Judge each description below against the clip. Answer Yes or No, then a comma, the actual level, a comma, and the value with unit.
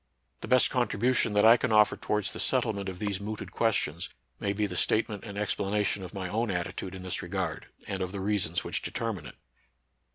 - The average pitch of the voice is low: Yes, low, 100 Hz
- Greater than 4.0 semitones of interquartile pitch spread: No, narrow, 2.4 semitones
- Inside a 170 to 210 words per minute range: Yes, average, 200 wpm